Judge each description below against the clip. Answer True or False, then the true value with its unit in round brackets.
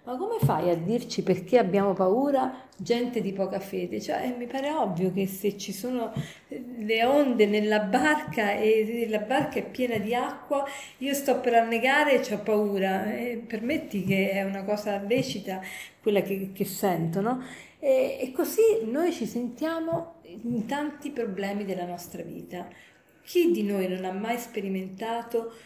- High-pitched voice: True (225 Hz)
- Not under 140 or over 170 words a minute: True (160 wpm)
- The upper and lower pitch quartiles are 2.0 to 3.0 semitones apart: False (4.7 semitones)